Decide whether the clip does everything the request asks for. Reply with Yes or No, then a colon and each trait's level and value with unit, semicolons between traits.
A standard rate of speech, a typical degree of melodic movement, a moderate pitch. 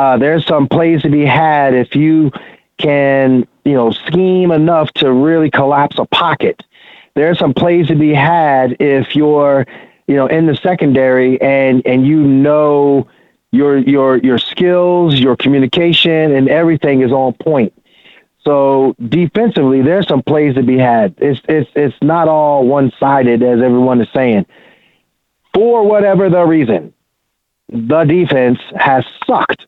Yes: average, 150 wpm; average, 3.3 semitones; medium, 145 Hz